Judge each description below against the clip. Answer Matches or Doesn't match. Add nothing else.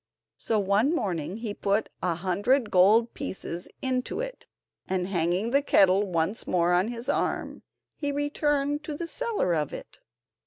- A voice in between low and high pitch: Doesn't match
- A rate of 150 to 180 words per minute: Matches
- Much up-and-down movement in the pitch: Matches